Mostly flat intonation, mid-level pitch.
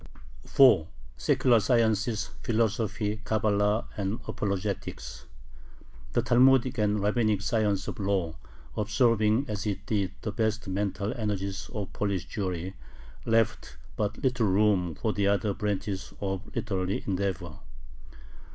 No: narrow, 2.1 semitones; low, 105 Hz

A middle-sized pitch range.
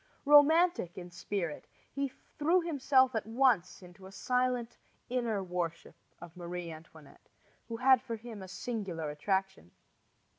No: wide, 6.4 semitones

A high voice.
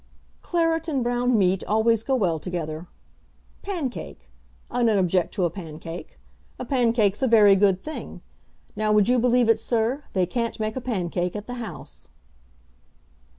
Yes: high, 220 Hz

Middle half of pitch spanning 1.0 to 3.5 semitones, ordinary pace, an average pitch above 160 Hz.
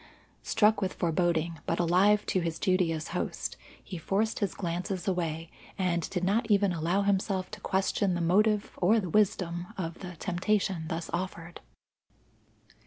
Yes: average, 2.9 semitones; average, 155 wpm; medium, 185 Hz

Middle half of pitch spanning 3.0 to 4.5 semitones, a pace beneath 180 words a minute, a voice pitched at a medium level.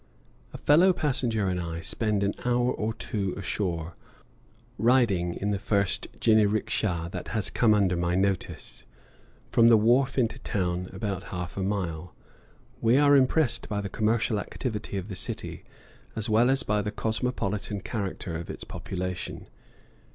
No: average, 3.8 semitones; average, 150 wpm; low, 105 Hz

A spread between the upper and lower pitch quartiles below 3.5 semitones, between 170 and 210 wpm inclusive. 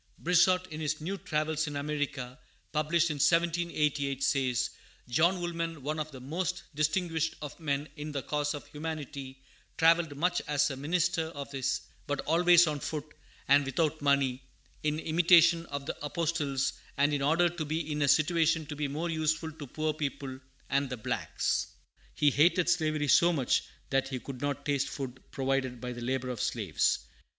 Yes: average, 2.9 semitones; average, 175 wpm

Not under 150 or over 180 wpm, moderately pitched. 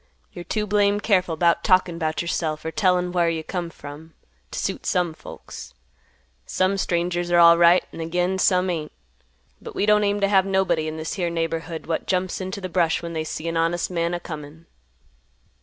No: average, 190 wpm; medium, 175 Hz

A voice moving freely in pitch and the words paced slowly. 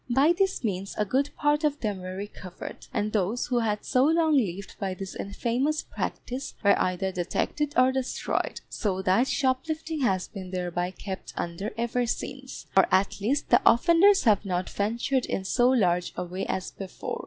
No: wide, 5.8 semitones; average, 175 wpm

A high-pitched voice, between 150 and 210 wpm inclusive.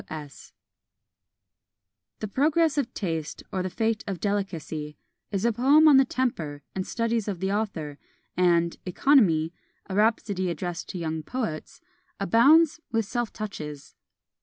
No: high, 195 Hz; average, 140 wpm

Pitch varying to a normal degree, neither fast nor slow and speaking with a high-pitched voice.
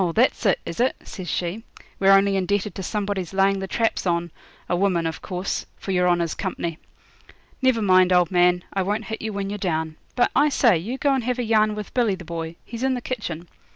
No: average, 3.8 semitones; fast, 220 wpm; high, 195 Hz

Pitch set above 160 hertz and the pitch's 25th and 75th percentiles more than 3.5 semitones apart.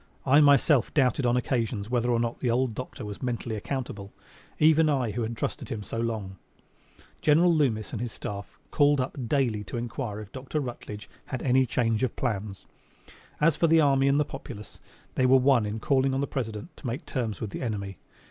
No: low, 125 Hz; average, 3.9 semitones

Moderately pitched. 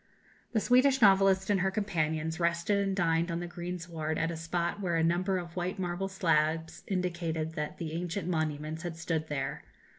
Yes: medium, 170 Hz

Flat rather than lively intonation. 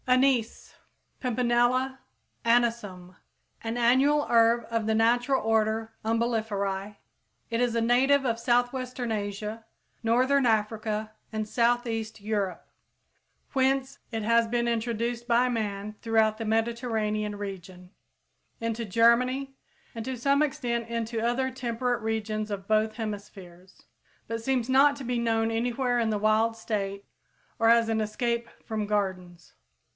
Yes: narrow, 2.1 semitones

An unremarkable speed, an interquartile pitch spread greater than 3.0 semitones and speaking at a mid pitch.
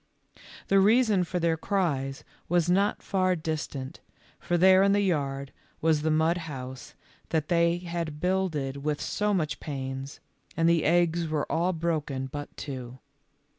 Yes: average, 150 wpm; average, 3.8 semitones; medium, 165 Hz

